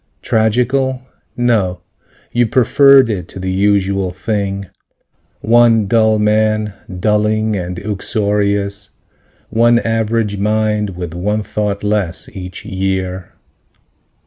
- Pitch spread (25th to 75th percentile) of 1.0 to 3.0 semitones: Yes, narrow, 2.4 semitones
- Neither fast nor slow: No, slow, 100 wpm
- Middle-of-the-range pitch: No, low, 105 Hz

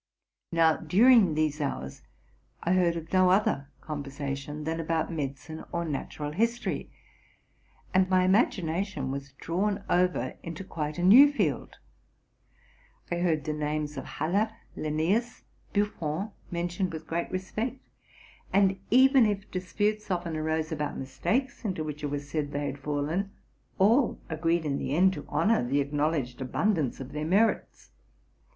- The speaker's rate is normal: Yes, average, 145 wpm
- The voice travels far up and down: No, average, 4.5 semitones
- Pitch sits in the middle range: Yes, medium, 165 Hz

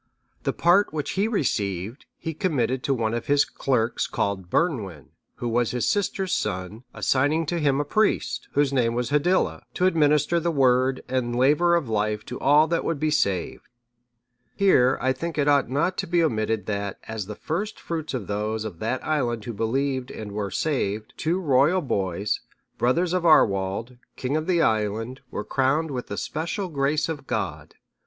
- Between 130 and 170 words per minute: No, average, 180 wpm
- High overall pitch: No, low, 130 Hz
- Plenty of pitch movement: Yes, wide, 6.1 semitones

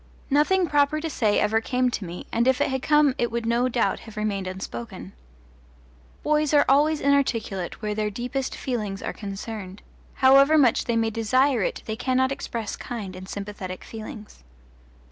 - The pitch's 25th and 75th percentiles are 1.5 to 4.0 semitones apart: No, average, 4.6 semitones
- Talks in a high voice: Yes, high, 235 Hz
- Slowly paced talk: No, average, 170 wpm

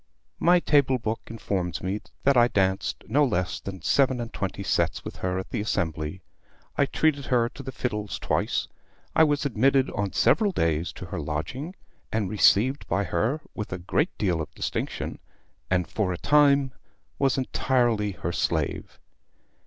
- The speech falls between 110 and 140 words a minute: No, average, 165 wpm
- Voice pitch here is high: No, low, 110 Hz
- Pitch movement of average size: No, wide, 6.8 semitones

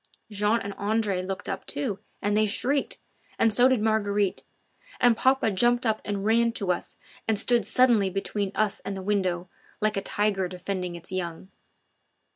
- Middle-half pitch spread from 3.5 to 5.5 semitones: No, narrow, 2.6 semitones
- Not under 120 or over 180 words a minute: Yes, average, 170 wpm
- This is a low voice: No, high, 205 Hz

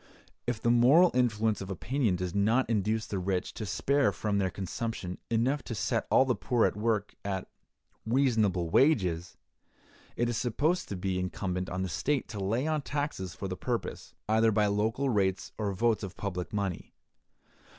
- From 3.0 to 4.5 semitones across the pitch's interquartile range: Yes, average, 4.2 semitones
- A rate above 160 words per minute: Yes, average, 175 wpm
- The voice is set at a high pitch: No, low, 105 Hz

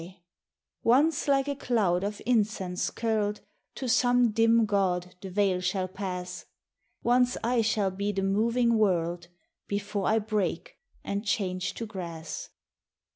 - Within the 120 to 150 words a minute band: Yes, average, 145 wpm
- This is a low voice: No, high, 205 Hz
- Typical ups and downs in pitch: Yes, average, 3.8 semitones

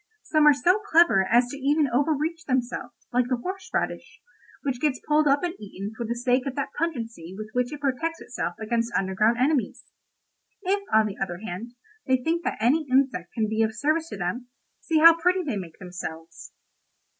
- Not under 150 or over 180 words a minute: No, average, 190 wpm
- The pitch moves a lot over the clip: Yes, wide, 5.8 semitones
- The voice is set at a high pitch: Yes, very high, 250 Hz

